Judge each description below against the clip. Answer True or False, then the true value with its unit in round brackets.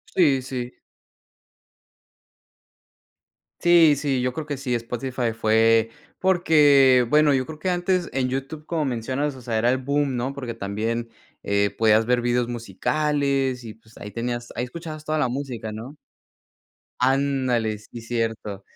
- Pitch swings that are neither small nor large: True (3.8 semitones)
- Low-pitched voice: True (125 Hz)